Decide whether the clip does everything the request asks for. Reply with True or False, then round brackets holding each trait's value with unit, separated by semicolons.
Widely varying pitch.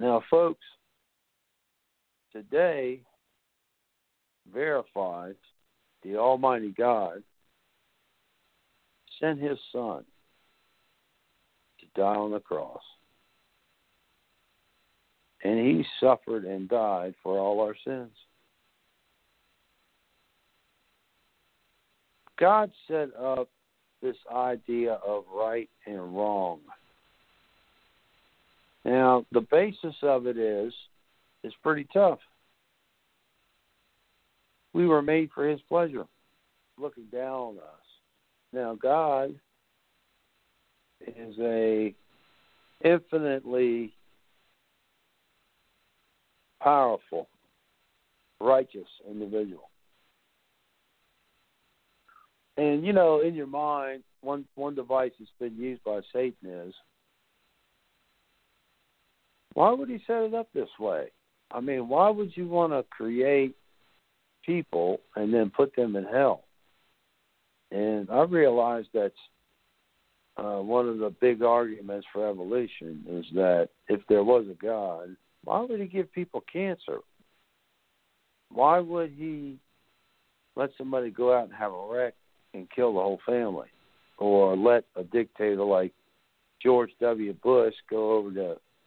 True (5.8 semitones)